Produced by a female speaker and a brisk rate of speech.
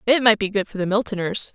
Yes: female; fast, 270 wpm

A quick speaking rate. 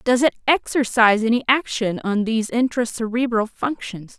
No: average, 145 wpm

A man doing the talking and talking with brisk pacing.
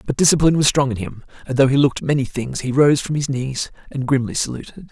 Yes: male; fast, 245 wpm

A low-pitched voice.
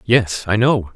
Yes: low, 105 Hz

